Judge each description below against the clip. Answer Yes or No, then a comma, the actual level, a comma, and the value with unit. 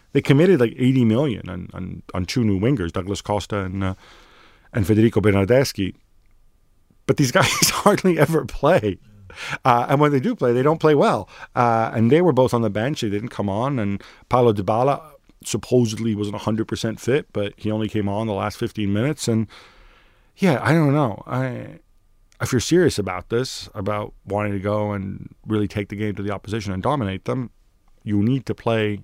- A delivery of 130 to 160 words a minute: No, average, 195 wpm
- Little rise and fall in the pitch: No, average, 3.8 semitones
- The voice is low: Yes, low, 110 Hz